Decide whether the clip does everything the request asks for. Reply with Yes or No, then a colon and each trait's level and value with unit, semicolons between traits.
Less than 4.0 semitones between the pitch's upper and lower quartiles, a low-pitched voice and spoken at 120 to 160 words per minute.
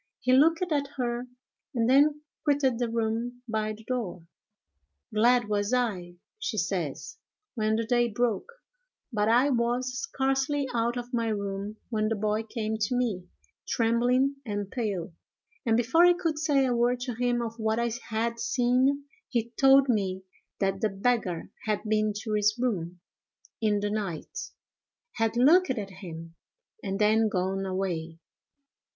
No: average, 3.2 semitones; high, 230 Hz; average, 155 wpm